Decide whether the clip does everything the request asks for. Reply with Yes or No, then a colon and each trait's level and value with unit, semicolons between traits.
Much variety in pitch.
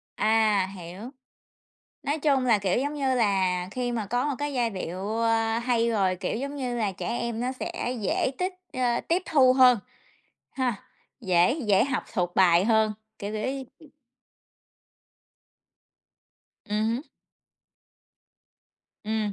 No: average, 4.0 semitones